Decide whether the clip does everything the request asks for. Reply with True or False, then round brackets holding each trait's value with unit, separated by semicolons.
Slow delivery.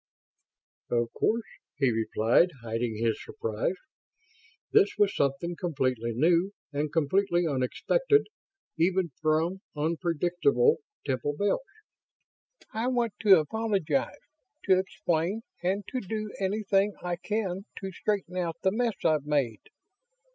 True (115 wpm)